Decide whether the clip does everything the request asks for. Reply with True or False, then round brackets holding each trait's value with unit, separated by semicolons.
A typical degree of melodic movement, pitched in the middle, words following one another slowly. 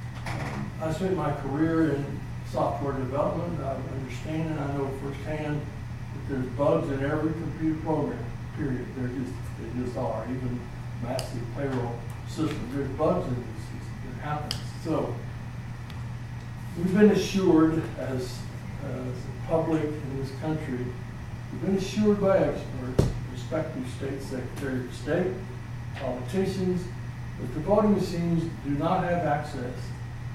False (4.2 semitones; 130 Hz; 130 wpm)